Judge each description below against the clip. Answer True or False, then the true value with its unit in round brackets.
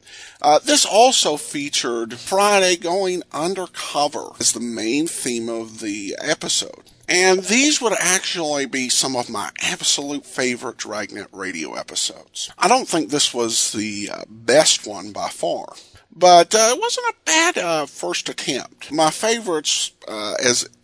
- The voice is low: False (170 Hz)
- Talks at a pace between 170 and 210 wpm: False (145 wpm)